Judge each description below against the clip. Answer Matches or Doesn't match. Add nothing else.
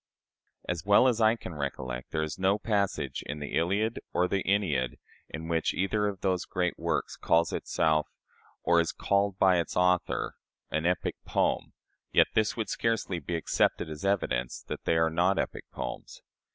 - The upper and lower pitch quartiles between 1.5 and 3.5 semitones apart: Doesn't match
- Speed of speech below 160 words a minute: Doesn't match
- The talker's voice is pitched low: Matches